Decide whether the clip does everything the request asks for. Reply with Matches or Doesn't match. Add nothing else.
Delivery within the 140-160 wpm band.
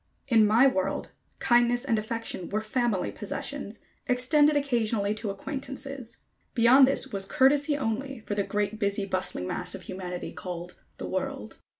Matches